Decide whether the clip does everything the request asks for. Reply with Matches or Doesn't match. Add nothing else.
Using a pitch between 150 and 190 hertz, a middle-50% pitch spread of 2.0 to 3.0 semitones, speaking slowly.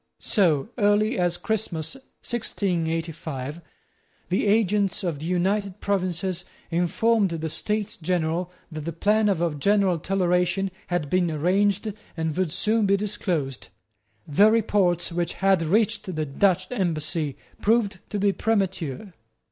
Doesn't match